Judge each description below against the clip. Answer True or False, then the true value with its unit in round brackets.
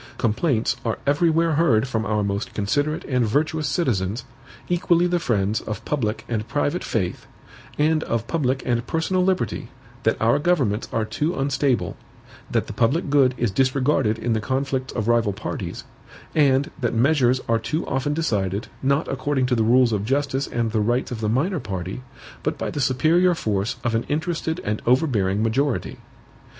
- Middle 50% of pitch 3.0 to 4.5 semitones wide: False (4.9 semitones)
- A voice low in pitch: True (130 Hz)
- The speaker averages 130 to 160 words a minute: False (170 wpm)